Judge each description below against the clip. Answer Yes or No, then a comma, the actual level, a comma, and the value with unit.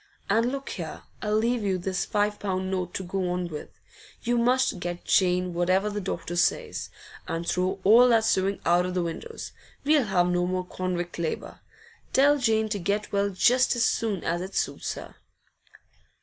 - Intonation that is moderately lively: Yes, average, 3.8 semitones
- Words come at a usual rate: Yes, average, 180 wpm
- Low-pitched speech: No, high, 190 Hz